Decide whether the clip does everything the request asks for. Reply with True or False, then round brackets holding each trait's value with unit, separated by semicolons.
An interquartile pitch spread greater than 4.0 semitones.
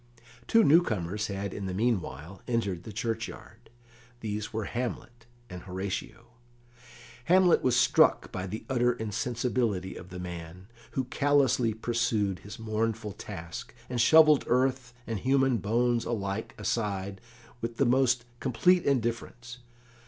False (3.7 semitones)